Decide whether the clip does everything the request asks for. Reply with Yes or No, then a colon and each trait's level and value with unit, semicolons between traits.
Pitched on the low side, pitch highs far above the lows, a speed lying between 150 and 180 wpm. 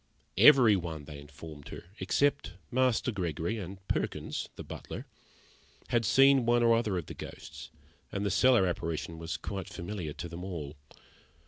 Yes: very low, 95 Hz; wide, 6.1 semitones; average, 155 wpm